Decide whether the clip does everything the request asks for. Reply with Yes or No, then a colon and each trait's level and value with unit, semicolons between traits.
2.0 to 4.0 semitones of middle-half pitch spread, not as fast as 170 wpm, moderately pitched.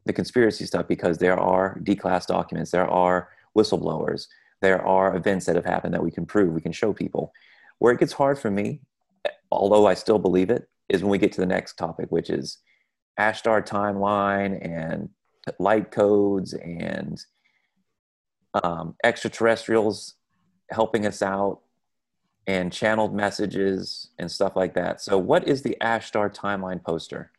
No: average, 2.7 semitones; average, 160 wpm; low, 100 Hz